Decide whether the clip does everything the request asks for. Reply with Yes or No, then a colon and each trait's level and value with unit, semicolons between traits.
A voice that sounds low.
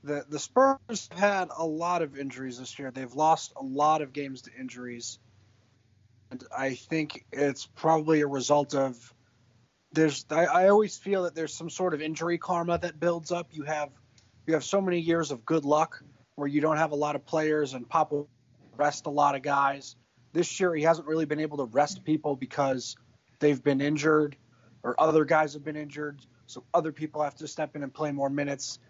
No: medium, 150 Hz